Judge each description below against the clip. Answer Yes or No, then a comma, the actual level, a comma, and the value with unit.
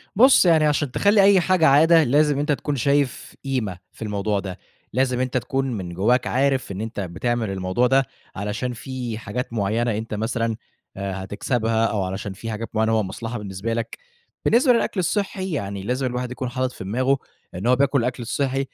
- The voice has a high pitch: No, low, 120 Hz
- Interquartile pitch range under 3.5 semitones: No, average, 4.5 semitones